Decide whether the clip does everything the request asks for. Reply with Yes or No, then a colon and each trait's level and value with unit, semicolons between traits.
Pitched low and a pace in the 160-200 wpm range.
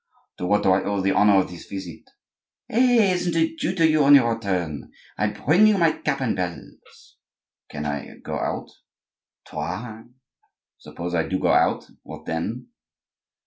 Yes: low, 105 Hz; average, 170 wpm